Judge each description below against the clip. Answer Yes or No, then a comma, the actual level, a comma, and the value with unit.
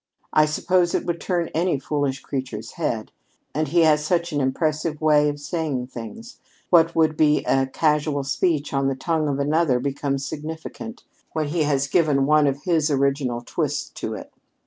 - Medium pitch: Yes, medium, 150 Hz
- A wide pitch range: No, average, 2.8 semitones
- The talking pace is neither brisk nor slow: Yes, average, 175 wpm